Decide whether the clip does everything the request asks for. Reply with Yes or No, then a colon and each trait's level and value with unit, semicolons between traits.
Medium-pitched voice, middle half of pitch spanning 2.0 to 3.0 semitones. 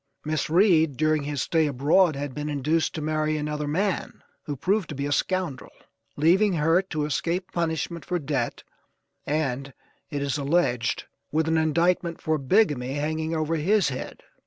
Yes: medium, 155 Hz; average, 2.7 semitones